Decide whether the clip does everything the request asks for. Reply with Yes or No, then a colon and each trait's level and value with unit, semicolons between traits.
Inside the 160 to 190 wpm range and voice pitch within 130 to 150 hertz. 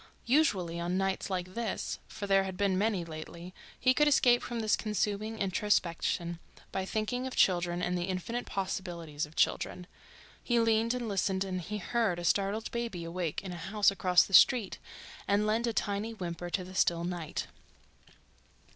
No: average, 170 wpm; high, 195 Hz